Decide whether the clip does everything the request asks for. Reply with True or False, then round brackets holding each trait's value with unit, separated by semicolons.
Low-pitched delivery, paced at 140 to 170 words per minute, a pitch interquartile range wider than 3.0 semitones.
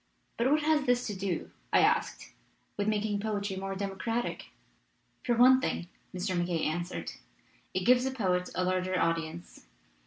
False (195 Hz; 155 wpm; 4.9 semitones)